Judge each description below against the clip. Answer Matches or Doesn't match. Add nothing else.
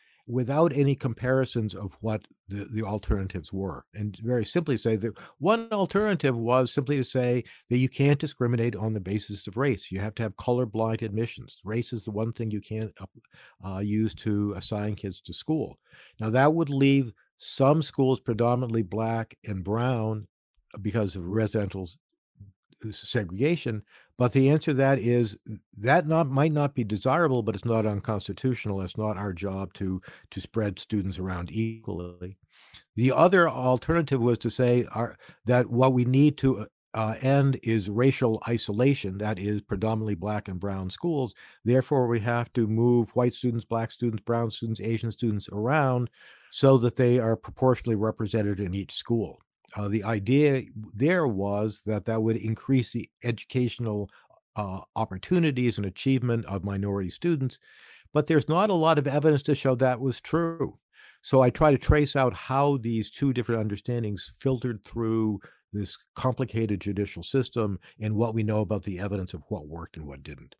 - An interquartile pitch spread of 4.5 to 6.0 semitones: Doesn't match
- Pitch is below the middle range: Matches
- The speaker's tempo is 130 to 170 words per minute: Matches